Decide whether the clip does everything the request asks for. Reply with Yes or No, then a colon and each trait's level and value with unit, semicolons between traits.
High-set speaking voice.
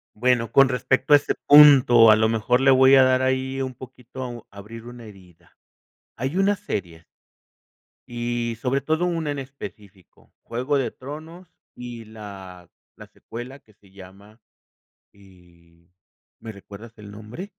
No: low, 120 Hz